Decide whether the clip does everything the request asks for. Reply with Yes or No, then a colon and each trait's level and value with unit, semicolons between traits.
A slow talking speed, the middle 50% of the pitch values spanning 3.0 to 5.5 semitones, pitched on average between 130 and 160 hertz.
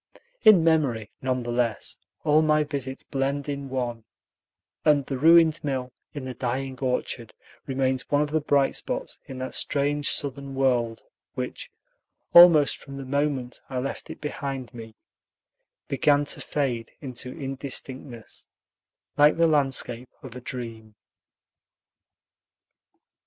No: slow, 130 wpm; narrow, 2.4 semitones; low, 135 Hz